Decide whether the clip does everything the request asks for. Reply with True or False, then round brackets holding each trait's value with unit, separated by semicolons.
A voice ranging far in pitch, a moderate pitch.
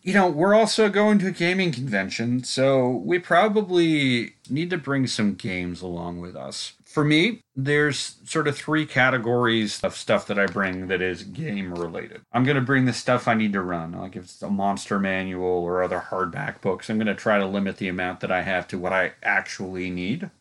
False (8.1 semitones; 120 Hz)